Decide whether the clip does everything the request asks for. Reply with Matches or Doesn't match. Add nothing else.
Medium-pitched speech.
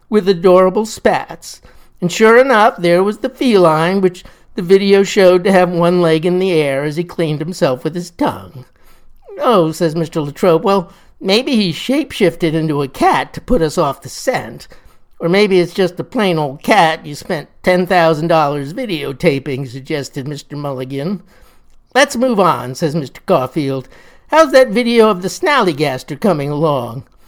Matches